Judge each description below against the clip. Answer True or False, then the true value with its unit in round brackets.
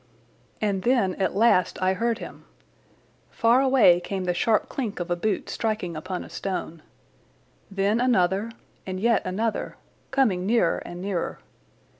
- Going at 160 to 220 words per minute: False (145 wpm)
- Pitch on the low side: False (195 Hz)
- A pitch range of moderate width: True (3.8 semitones)